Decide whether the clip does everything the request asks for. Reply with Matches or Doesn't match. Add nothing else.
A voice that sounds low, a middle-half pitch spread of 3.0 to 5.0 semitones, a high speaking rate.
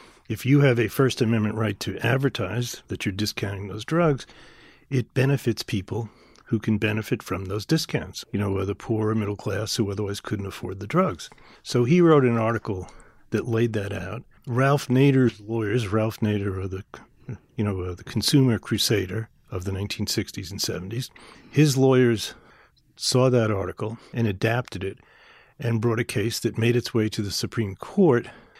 Doesn't match